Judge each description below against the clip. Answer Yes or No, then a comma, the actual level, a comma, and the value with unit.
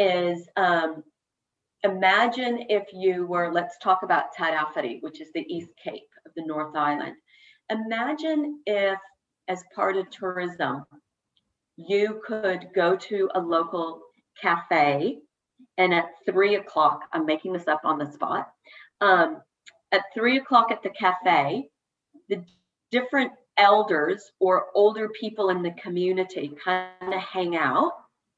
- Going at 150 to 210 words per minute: No, slow, 135 wpm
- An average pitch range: Yes, average, 3.7 semitones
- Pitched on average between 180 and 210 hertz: Yes, high, 190 Hz